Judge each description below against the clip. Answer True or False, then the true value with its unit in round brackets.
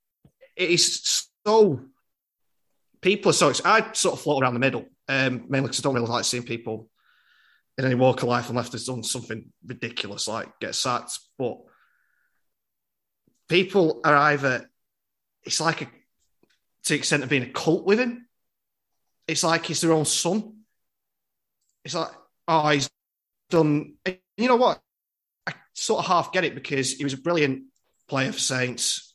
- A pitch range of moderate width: True (5.0 semitones)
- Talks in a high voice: False (140 Hz)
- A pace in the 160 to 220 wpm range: True (165 wpm)